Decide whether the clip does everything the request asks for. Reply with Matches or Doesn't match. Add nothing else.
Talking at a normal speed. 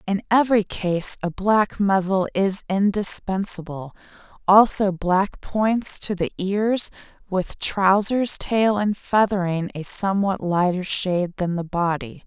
Doesn't match